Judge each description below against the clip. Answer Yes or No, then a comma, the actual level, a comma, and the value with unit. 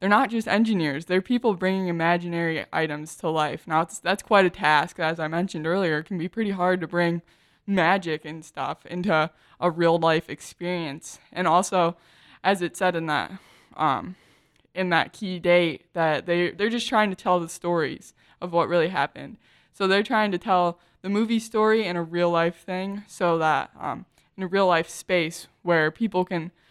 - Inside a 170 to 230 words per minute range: Yes, average, 190 wpm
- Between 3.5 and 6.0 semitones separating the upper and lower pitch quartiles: No, average, 2.7 semitones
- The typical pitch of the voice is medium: Yes, medium, 175 Hz